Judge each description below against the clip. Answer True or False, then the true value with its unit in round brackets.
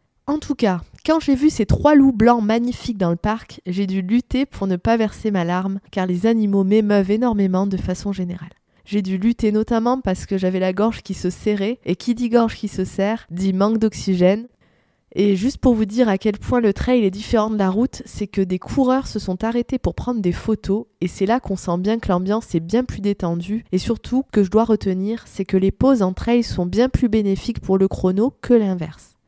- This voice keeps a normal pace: False (230 wpm)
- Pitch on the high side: True (210 Hz)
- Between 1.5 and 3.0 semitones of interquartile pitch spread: False (3.7 semitones)